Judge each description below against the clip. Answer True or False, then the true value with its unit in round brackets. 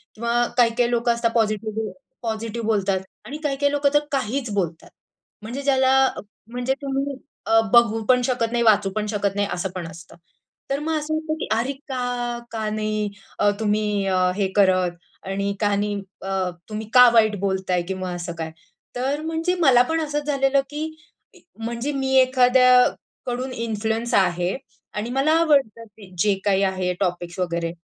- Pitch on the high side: True (225 Hz)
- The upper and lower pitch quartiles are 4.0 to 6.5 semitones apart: True (4.7 semitones)